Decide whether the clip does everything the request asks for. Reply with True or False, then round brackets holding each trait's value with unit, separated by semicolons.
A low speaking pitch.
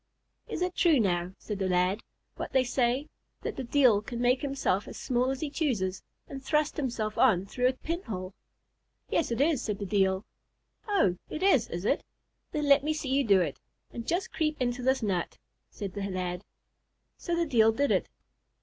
False (245 Hz)